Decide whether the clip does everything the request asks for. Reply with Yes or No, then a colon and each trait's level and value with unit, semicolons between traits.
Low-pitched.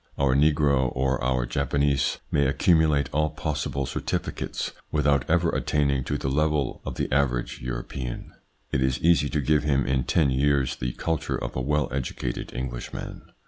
Yes: very low, 70 Hz